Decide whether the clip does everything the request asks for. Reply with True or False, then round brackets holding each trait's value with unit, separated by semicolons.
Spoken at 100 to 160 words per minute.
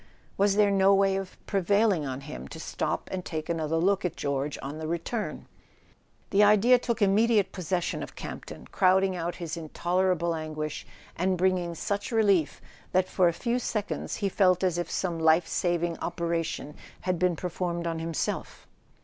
False (175 wpm)